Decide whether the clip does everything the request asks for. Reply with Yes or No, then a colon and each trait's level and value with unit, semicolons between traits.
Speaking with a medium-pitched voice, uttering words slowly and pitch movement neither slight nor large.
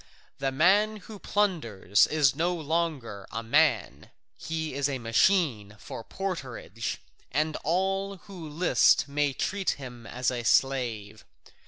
No: medium, 145 Hz; slow, 130 wpm; wide, 7.0 semitones